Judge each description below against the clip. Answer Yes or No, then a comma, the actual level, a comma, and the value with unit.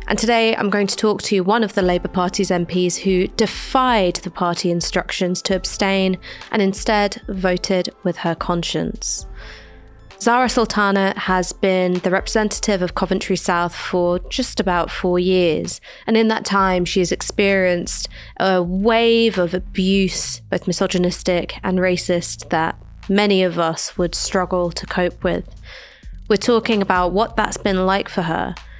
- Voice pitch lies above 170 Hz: Yes, medium, 185 Hz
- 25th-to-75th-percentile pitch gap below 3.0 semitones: Yes, narrow, 2.5 semitones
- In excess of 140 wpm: Yes, average, 150 wpm